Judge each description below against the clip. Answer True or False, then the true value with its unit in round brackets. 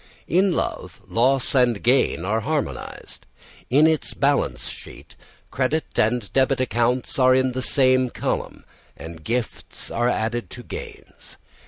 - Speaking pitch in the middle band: False (130 Hz)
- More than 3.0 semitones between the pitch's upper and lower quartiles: False (2.5 semitones)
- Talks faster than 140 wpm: False (135 wpm)